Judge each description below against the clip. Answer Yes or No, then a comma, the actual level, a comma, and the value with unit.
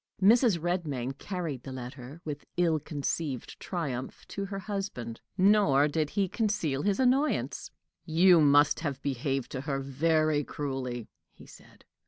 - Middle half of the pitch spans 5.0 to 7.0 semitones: Yes, wide, 5.4 semitones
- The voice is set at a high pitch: No, medium, 150 Hz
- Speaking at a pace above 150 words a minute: No, average, 140 wpm